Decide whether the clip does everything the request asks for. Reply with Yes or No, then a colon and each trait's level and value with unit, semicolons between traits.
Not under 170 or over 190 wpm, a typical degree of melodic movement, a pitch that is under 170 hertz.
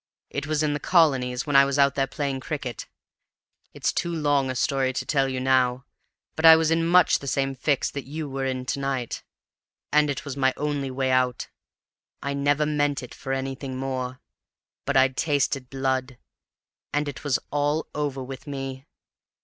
No: average, 185 wpm; narrow, 1.9 semitones; low, 135 Hz